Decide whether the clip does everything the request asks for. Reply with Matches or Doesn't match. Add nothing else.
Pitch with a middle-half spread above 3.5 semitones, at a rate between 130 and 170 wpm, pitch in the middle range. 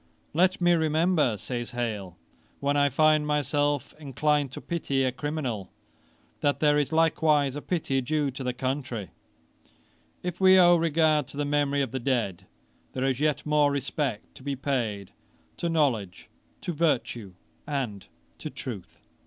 Doesn't match